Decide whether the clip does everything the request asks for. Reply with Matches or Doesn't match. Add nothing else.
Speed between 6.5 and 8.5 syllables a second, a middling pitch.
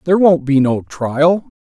Doesn't match